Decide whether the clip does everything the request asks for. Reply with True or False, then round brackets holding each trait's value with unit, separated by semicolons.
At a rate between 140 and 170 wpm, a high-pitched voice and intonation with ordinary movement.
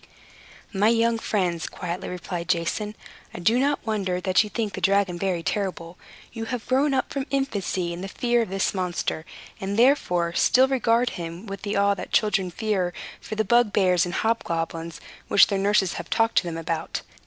False (185 wpm; 195 Hz; 4.3 semitones)